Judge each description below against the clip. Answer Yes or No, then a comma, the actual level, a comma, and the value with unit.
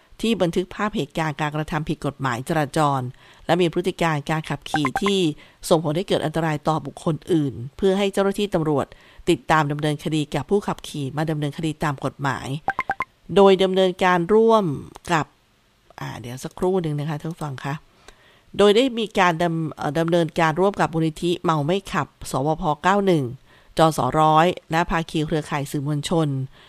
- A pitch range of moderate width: Yes, average, 3.5 semitones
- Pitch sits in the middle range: Yes, medium, 160 Hz